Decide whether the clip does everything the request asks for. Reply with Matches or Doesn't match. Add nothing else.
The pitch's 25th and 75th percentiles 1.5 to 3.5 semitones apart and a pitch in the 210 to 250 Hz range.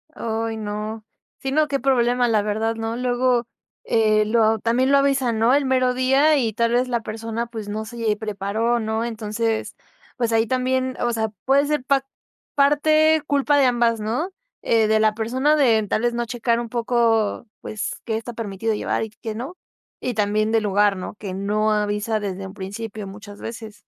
Matches